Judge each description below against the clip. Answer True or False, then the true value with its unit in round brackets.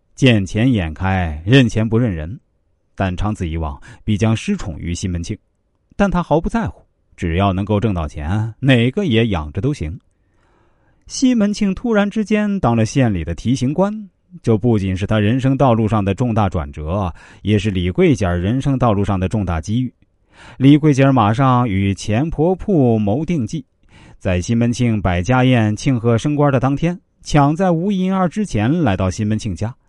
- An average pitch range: False (5.9 semitones)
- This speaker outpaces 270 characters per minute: False (255 characters per minute)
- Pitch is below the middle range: True (110 Hz)